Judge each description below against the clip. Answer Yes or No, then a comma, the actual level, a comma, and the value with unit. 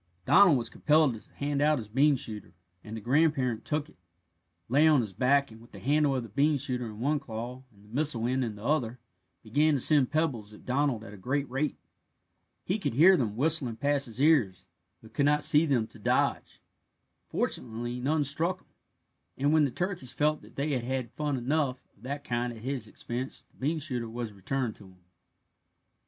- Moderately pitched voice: No, low, 130 Hz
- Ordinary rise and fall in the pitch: Yes, average, 4.2 semitones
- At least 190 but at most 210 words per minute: Yes, fast, 205 wpm